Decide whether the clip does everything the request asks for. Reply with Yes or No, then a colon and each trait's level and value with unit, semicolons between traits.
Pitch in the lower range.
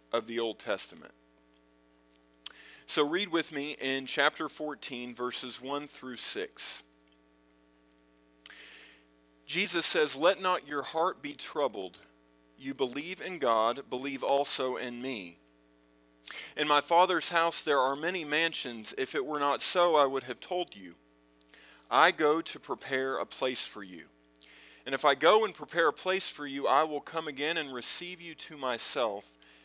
Yes: low, 125 Hz